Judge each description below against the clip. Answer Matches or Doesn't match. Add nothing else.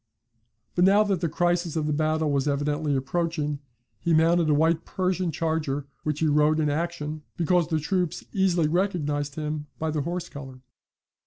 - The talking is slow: Doesn't match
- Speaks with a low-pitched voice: Doesn't match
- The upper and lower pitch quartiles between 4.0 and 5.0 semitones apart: Doesn't match